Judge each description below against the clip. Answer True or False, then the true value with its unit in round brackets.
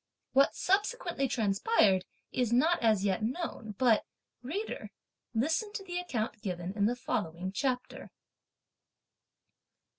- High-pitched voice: True (245 Hz)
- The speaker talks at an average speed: False (115 wpm)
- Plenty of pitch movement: True (8.3 semitones)